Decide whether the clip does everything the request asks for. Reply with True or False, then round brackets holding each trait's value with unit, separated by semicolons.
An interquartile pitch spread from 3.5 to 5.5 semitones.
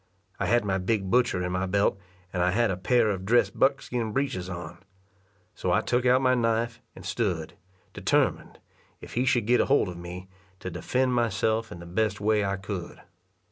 True (4.6 semitones)